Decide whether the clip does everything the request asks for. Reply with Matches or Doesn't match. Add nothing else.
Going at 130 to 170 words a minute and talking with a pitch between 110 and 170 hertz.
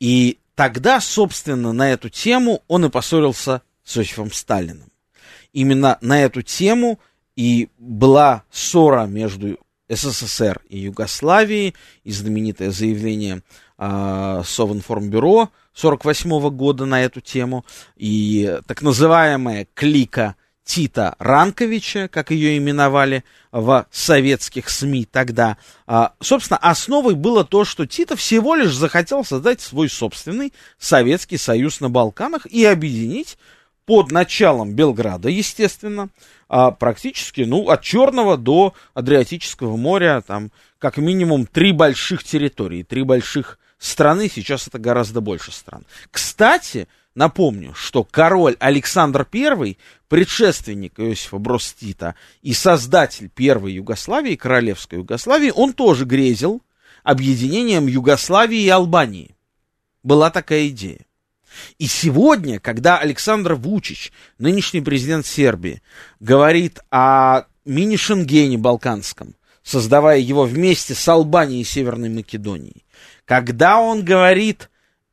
Doesn't match